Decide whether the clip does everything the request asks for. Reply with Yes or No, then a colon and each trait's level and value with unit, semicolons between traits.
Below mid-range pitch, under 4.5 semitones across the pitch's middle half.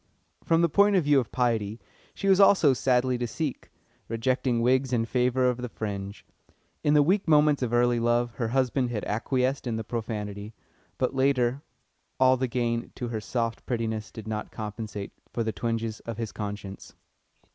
Yes: low, 120 Hz; average, 2.8 semitones